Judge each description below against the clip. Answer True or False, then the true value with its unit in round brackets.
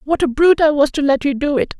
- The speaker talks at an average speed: False (335 wpm)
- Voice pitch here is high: True (290 Hz)